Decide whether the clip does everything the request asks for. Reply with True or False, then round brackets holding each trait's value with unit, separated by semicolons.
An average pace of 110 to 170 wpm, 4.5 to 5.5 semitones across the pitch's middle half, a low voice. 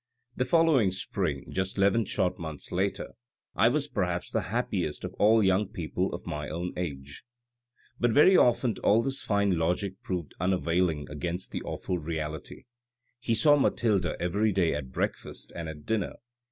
True (160 wpm; 4.8 semitones; 95 Hz)